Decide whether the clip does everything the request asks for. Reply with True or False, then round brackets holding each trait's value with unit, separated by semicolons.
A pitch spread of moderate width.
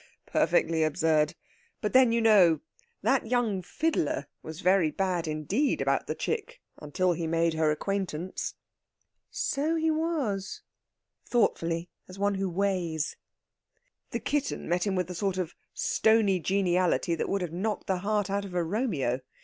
True (4.4 semitones)